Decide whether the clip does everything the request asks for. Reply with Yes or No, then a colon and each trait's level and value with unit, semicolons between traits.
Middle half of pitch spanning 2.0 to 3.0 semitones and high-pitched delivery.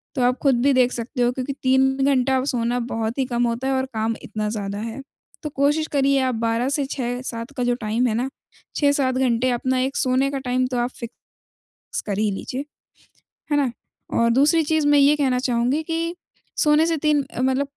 Yes: average, 2.7 semitones; very high, 255 Hz